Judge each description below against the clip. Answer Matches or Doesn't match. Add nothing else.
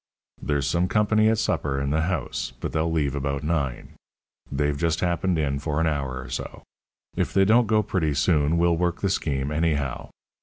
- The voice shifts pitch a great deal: Doesn't match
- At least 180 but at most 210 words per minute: Matches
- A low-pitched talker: Matches